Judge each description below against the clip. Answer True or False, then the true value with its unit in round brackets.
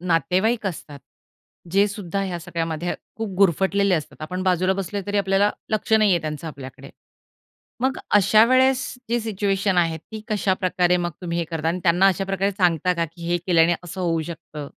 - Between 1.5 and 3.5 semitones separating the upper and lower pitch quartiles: True (3.1 semitones)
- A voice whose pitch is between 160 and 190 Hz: True (185 Hz)